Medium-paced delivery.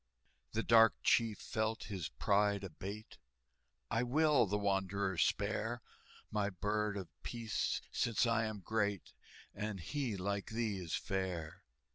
No: slow, 130 wpm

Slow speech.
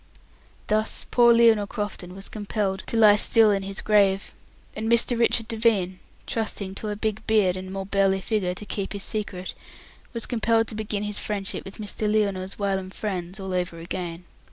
No: average, 180 wpm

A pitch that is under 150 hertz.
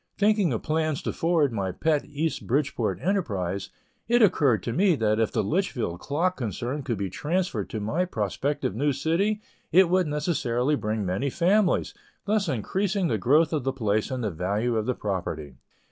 Yes: medium, 140 Hz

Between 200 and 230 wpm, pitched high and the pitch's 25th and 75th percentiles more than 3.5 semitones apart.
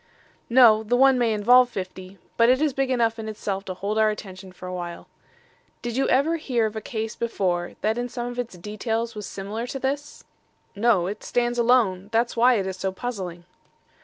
Yes: fast, 205 wpm; high, 225 Hz; average, 4.0 semitones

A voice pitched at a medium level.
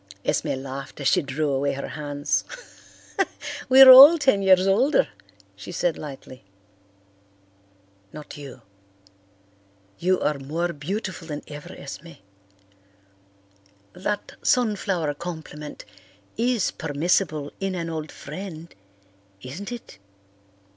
Yes: medium, 165 Hz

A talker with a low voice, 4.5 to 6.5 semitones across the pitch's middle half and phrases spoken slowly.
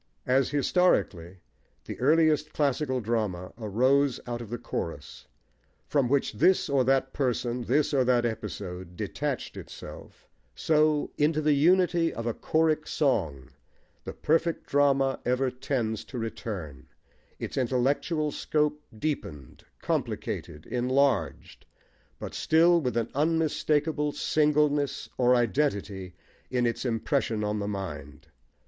Yes: low, 130 Hz; average, 5.2 semitones; slow, 120 wpm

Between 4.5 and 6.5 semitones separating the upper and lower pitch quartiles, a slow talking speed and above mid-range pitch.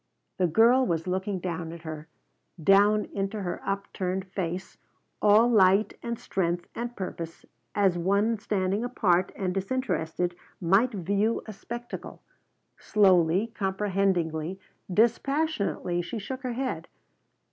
No: average, 3.7 semitones; slow, 120 wpm; high, 195 Hz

